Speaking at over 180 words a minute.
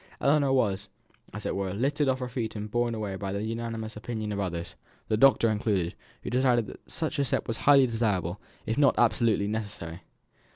Yes: average, 195 wpm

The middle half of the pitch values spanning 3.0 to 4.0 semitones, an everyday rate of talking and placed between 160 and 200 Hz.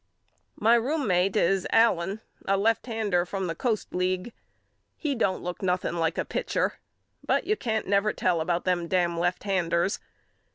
Yes: average, 3.7 semitones; average, 155 wpm; high, 190 Hz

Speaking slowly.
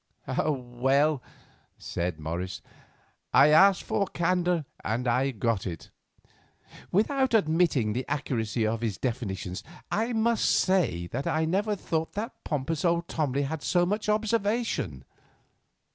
Yes: slow, 130 wpm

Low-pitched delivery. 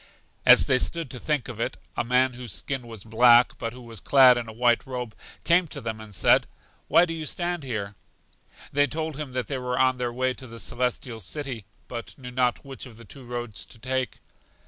Yes: low, 125 Hz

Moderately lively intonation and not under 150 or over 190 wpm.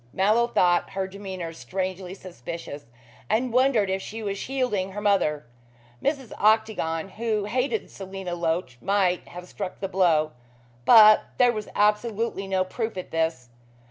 No: average, 3.5 semitones; average, 140 wpm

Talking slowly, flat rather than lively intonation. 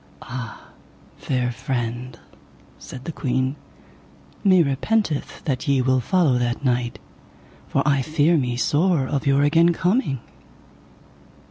No: slow, 120 wpm; average, 3.9 semitones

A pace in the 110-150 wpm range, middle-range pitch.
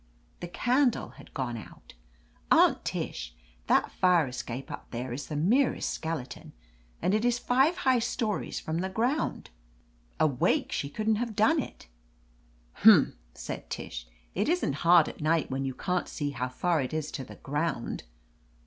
No: average, 160 wpm; medium, 165 Hz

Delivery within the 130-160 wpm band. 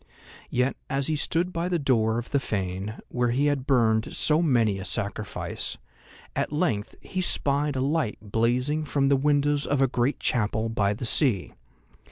No: average, 175 wpm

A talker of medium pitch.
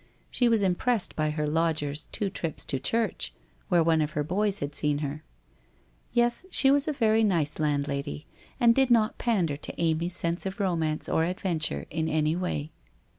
Yes: medium, 165 Hz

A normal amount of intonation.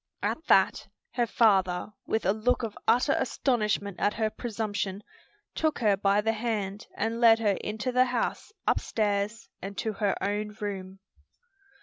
No: narrow, 2.2 semitones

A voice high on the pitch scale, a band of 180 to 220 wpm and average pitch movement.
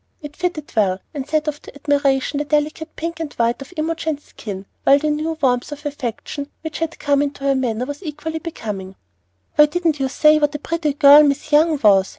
No: very high, 295 Hz; fast, 205 wpm; narrow, 2.2 semitones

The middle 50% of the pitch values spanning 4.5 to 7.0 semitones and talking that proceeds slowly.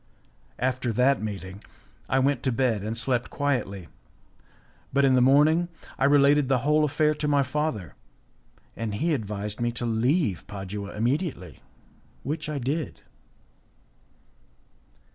Yes: average, 5.0 semitones; slow, 130 wpm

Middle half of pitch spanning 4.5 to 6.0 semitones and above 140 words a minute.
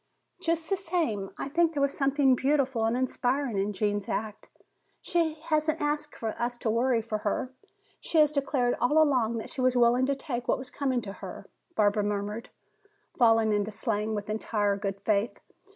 Yes: average, 4.8 semitones; average, 180 wpm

